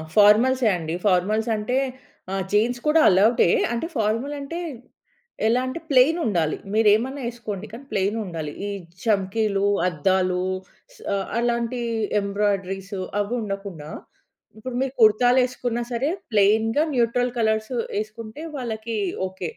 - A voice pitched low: No, high, 220 Hz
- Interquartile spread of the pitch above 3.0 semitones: Yes, average, 3.5 semitones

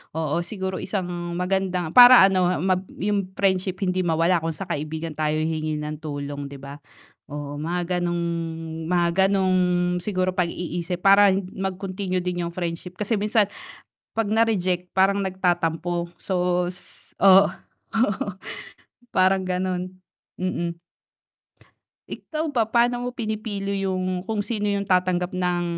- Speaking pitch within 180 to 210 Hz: Yes, medium, 185 Hz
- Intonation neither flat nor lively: No, narrow, 2.2 semitones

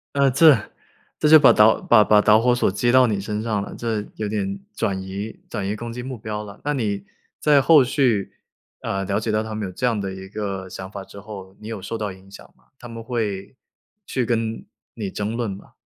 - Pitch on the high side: No, low, 105 Hz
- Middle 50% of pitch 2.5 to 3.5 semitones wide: Yes, average, 3.1 semitones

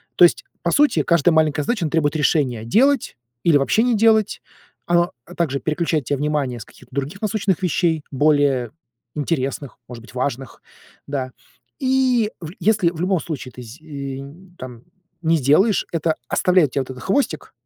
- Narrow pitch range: No, average, 5.0 semitones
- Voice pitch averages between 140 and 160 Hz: Yes, medium, 155 Hz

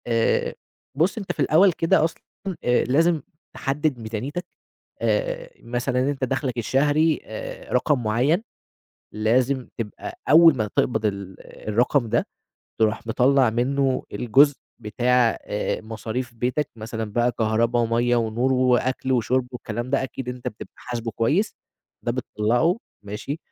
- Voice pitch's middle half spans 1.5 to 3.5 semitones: No, average, 3.9 semitones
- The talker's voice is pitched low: Yes, low, 125 Hz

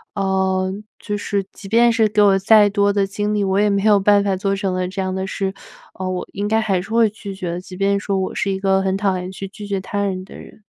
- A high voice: Yes, high, 195 Hz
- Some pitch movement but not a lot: No, narrow, 1.4 semitones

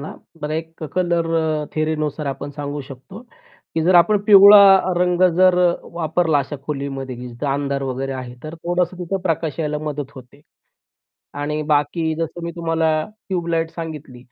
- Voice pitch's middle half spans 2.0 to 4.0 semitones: Yes, average, 3.5 semitones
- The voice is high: No, medium, 160 Hz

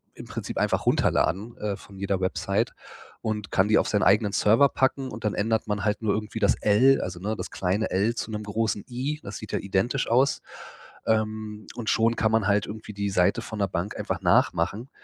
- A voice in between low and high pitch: No, low, 105 Hz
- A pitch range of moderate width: No, narrow, 1.8 semitones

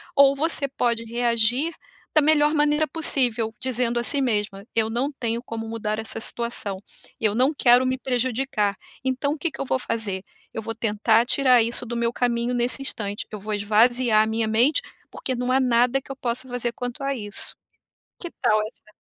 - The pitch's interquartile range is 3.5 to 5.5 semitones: No, average, 2.8 semitones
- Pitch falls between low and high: No, high, 240 Hz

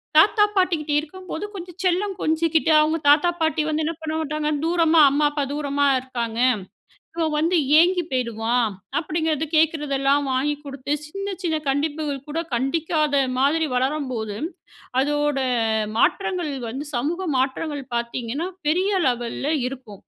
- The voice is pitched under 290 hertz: No, very high, 300 Hz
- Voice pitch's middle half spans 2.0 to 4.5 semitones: Yes, average, 3.3 semitones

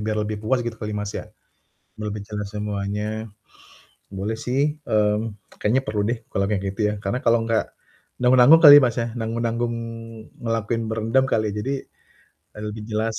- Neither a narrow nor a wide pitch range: No, narrow, 2.0 semitones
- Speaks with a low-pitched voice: Yes, low, 110 Hz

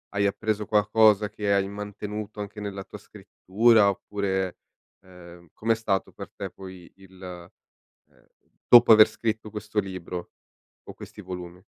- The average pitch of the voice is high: No, low, 100 Hz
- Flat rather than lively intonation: Yes, narrow, 2.3 semitones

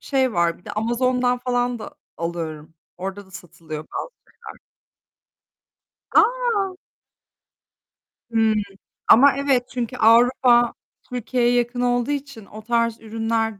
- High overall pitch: Yes, high, 240 Hz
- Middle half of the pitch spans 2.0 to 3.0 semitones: Yes, average, 2.7 semitones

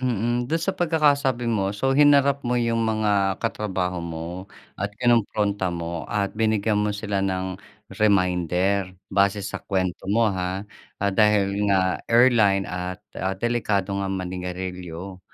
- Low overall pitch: Yes, low, 100 Hz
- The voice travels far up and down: No, average, 3.6 semitones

